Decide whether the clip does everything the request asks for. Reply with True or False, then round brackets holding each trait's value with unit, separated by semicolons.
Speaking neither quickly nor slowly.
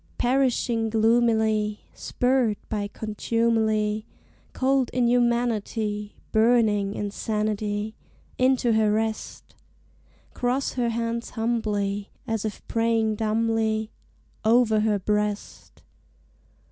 False (85 wpm)